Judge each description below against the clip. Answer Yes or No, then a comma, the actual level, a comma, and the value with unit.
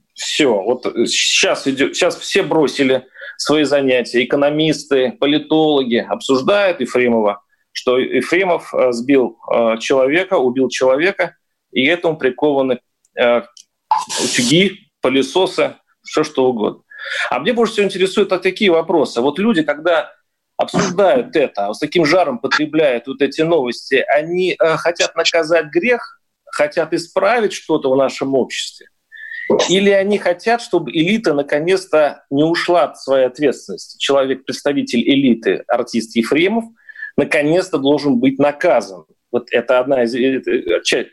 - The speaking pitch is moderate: Yes, medium, 155 Hz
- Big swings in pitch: Yes, wide, 6.6 semitones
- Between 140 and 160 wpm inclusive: No, average, 120 wpm